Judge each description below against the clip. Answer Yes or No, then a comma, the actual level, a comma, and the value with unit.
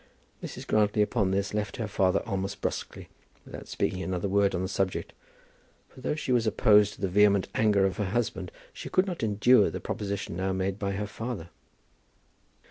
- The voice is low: Yes, low, 100 Hz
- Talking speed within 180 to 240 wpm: Yes, average, 185 wpm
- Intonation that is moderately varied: No, narrow, 2.0 semitones